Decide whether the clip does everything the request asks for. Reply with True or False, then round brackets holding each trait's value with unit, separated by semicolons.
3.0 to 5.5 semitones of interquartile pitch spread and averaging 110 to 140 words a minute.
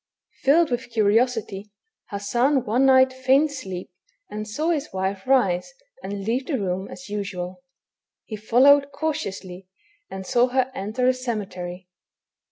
True (5.2 semitones; 135 wpm)